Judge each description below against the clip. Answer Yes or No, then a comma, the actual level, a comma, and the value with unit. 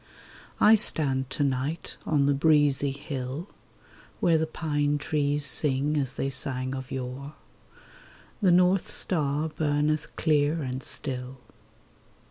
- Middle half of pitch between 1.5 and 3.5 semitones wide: Yes, narrow, 2.5 semitones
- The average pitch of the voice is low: No, medium, 145 Hz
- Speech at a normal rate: No, slow, 120 wpm